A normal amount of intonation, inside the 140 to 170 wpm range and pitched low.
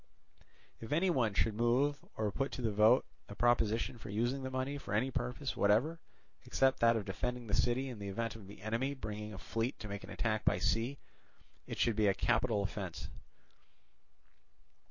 No: average, 3.7 semitones; average, 190 wpm; low, 115 Hz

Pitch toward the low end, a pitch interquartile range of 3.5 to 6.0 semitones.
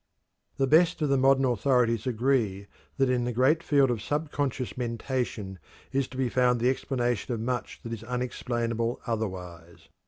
No: low, 125 Hz; narrow, 2.5 semitones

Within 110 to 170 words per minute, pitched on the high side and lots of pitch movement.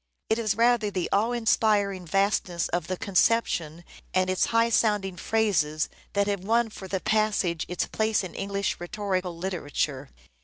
No: average, 160 wpm; high, 195 Hz; average, 3.4 semitones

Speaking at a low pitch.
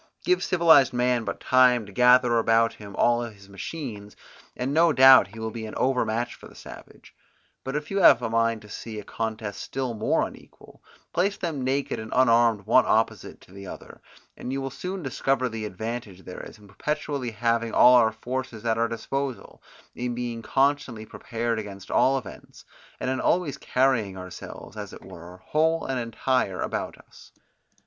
Yes: low, 120 Hz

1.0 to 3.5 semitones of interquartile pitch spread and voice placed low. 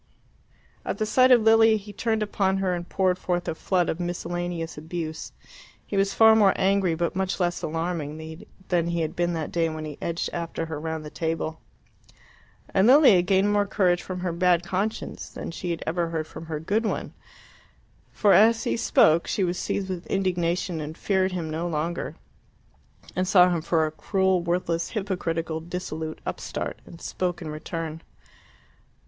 No: average, 2.8 semitones; medium, 175 Hz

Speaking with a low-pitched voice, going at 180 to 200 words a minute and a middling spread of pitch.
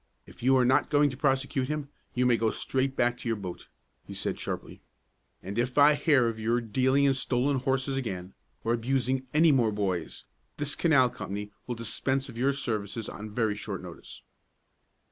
Yes: low, 125 Hz; average, 185 wpm; average, 3.2 semitones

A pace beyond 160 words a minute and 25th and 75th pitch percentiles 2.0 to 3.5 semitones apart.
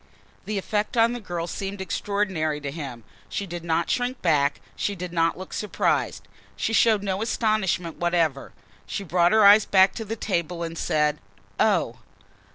No: average, 170 wpm; average, 3.9 semitones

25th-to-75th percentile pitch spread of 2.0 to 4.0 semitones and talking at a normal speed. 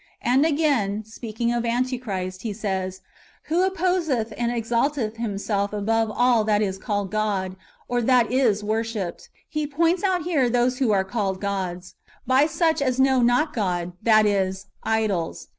No: average, 4.4 semitones; average, 160 wpm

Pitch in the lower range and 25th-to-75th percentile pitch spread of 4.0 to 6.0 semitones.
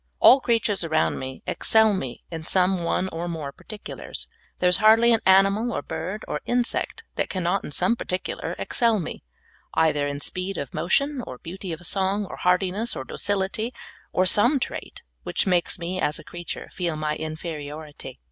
No: medium, 185 Hz; average, 4.7 semitones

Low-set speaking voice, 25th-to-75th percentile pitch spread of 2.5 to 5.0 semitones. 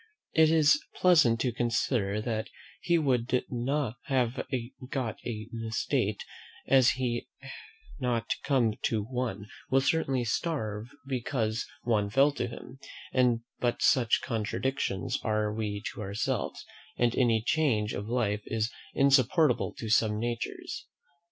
Yes: low, 120 Hz; average, 3.5 semitones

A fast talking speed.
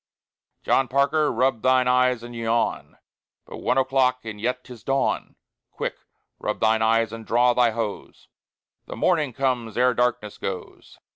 No: average, 150 wpm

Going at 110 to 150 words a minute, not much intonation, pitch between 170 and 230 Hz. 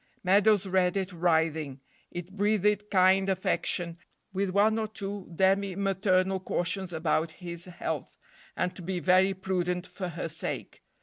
Yes: average, 140 wpm; narrow, 2.0 semitones; medium, 185 Hz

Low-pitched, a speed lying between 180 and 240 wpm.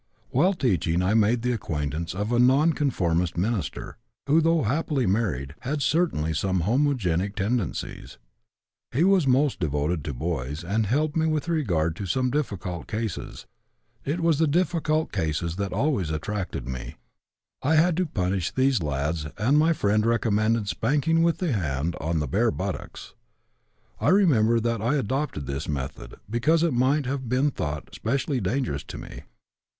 No: low, 115 Hz; average, 160 wpm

